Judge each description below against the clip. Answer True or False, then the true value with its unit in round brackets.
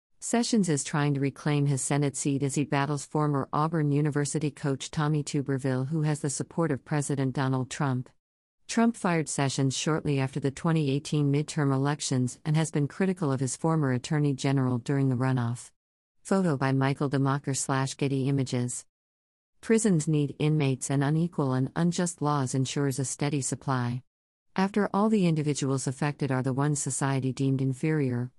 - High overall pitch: False (140 Hz)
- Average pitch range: False (2.2 semitones)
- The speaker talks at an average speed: True (160 wpm)